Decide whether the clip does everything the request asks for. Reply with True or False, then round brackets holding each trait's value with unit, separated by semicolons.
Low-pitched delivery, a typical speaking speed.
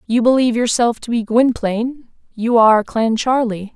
False (235 Hz; 145 wpm)